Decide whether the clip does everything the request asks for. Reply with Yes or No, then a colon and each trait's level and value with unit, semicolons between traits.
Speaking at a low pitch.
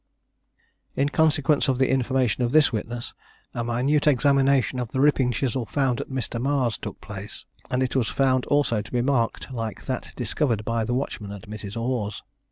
Yes: low, 125 Hz